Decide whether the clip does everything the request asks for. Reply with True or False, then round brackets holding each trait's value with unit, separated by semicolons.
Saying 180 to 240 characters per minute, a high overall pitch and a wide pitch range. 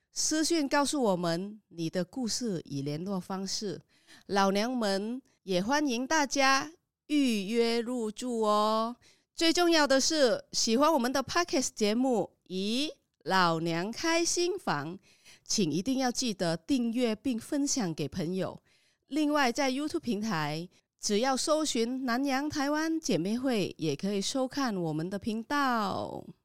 True (225 characters per minute; 235 Hz; 6.4 semitones)